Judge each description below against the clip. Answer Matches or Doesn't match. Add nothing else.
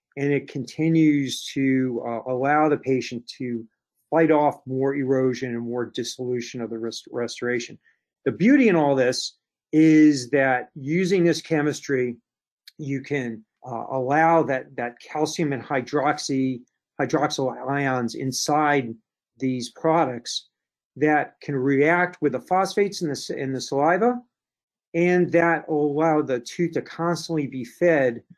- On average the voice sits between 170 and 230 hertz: Doesn't match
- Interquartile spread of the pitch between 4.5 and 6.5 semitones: Doesn't match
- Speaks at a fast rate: Doesn't match